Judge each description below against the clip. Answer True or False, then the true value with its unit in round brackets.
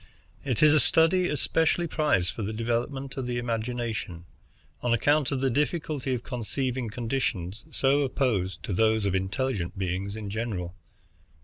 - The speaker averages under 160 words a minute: True (150 wpm)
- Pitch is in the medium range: False (120 Hz)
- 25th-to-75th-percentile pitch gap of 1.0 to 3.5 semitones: False (4.8 semitones)